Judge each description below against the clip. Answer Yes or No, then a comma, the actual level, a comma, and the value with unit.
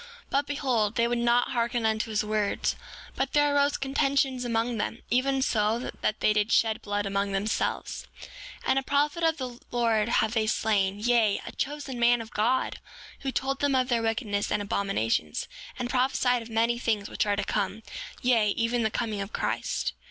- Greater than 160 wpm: Yes, average, 190 wpm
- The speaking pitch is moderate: No, high, 230 Hz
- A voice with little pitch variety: No, average, 3.2 semitones